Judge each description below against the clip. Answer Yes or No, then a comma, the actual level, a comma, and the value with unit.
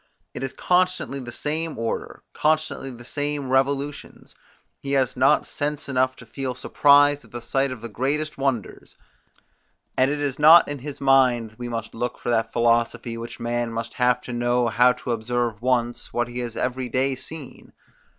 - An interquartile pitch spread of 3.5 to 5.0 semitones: No, average, 2.9 semitones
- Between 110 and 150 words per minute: No, average, 180 wpm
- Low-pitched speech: Yes, low, 130 Hz